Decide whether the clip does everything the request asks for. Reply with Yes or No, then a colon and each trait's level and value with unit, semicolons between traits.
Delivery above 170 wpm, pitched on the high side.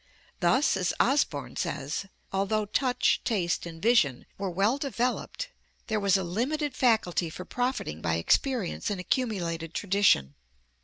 No: slow, 135 wpm; high, 200 Hz